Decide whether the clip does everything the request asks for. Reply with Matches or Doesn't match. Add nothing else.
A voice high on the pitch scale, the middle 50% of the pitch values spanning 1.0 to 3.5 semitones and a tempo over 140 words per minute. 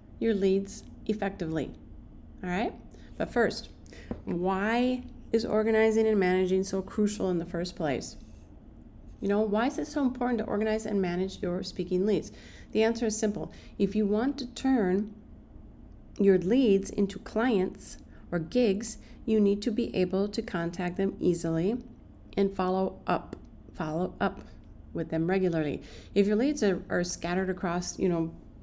Matches